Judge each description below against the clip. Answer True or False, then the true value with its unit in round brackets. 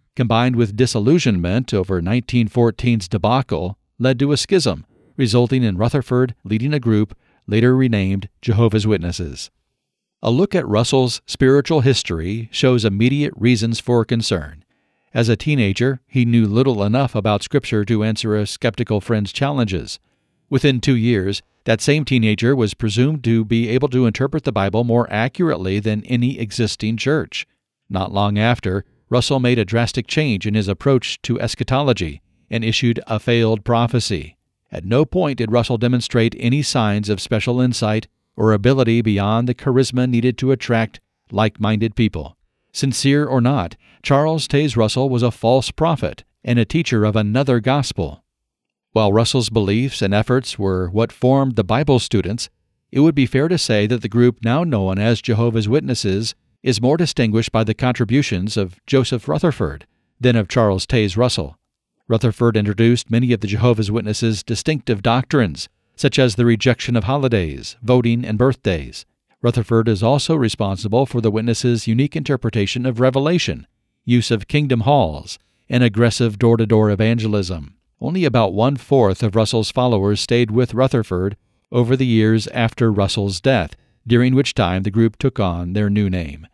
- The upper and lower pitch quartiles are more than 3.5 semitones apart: False (3.2 semitones)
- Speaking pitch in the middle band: False (115 Hz)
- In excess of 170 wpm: False (155 wpm)